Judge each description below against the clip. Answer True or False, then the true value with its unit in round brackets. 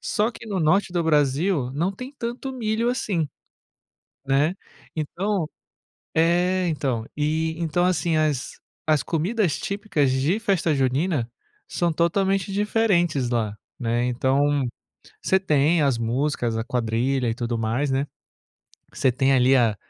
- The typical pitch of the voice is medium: True (155 Hz)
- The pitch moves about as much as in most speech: False (6.1 semitones)